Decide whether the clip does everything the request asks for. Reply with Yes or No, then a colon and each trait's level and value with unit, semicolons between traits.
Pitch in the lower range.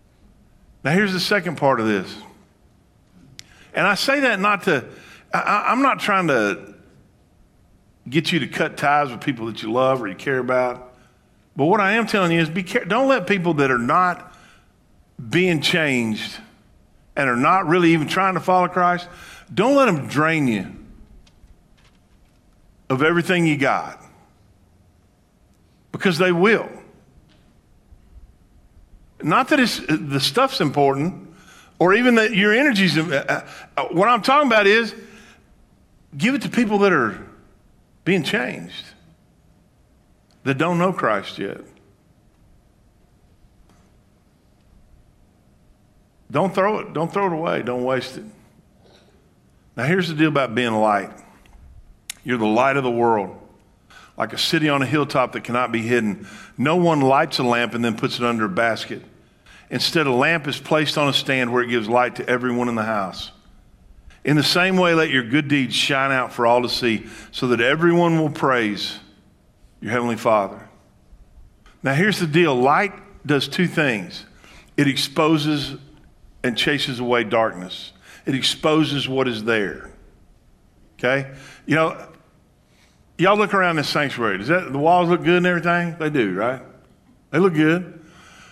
No: medium, 145 Hz